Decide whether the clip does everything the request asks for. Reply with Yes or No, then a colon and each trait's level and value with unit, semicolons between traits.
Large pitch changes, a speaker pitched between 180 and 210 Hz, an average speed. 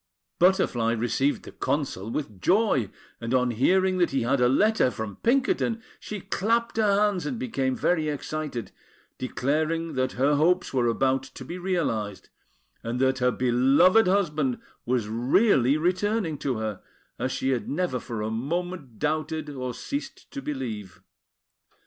No: wide, 6.6 semitones; medium, 140 Hz; average, 150 wpm